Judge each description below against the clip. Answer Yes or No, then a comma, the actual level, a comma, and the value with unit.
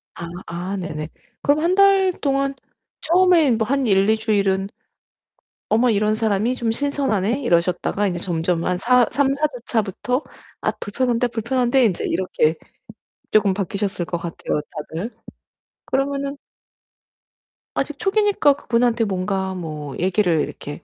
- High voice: Yes, high, 220 Hz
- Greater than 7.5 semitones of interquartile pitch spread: No, wide, 6.5 semitones